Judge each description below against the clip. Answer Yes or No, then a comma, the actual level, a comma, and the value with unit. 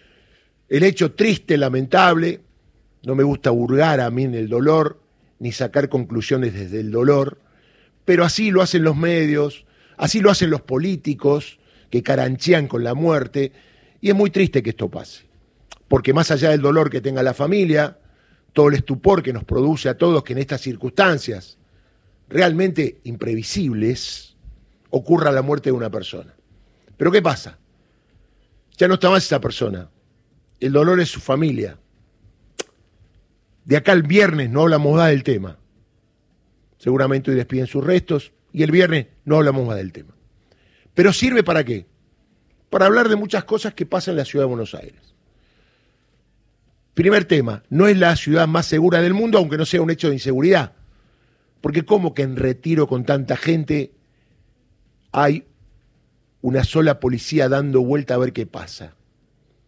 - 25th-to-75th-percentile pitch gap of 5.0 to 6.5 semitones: Yes, wide, 5.5 semitones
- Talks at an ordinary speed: Yes, average, 160 wpm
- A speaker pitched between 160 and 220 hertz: No, medium, 140 Hz